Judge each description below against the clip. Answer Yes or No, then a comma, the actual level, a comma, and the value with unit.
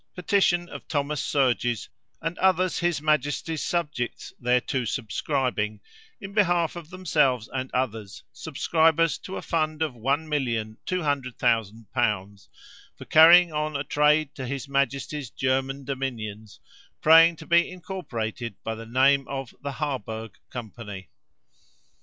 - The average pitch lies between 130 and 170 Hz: Yes, medium, 140 Hz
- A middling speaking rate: No, slow, 120 wpm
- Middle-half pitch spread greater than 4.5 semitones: Yes, average, 5.1 semitones